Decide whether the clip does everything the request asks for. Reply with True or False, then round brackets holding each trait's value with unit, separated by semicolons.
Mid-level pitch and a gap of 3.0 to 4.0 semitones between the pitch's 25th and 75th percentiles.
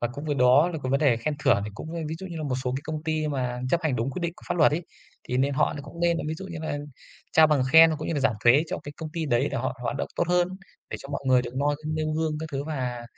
True (150 Hz; 3.6 semitones)